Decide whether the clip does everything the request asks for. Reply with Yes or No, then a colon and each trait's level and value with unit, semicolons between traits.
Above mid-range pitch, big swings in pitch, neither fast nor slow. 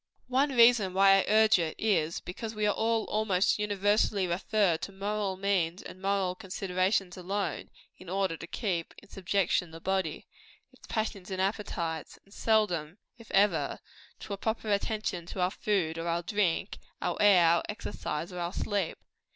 No: high, 195 Hz; average, 2.8 semitones; average, 165 wpm